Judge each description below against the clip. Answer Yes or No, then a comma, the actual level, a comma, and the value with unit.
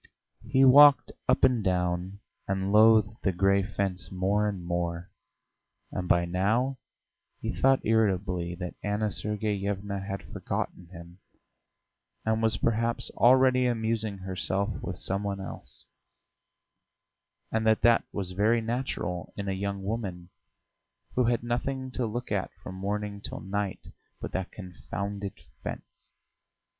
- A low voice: Yes, low, 100 Hz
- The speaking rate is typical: No, slow, 130 wpm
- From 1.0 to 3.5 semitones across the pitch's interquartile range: Yes, average, 3.1 semitones